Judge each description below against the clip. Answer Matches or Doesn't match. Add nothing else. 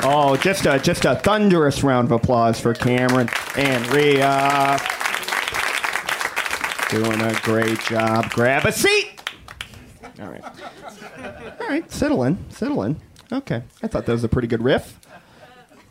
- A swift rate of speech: Doesn't match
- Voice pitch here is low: Matches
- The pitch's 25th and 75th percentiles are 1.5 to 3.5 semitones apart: Doesn't match